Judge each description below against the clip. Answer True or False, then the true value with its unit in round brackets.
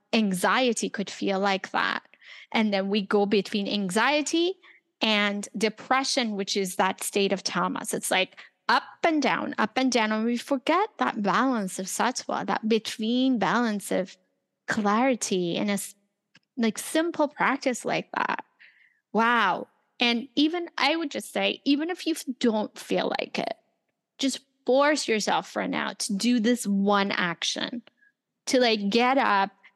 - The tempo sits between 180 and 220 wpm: False (150 wpm)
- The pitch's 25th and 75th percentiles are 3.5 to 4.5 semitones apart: False (5.0 semitones)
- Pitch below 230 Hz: False (235 Hz)